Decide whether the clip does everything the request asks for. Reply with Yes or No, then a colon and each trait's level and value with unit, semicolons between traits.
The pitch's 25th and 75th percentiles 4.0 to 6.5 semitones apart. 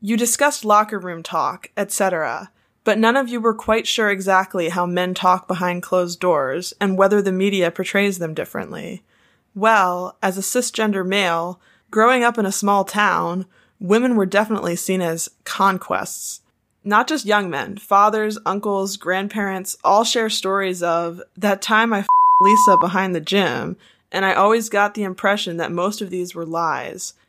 No: average, 2.8 semitones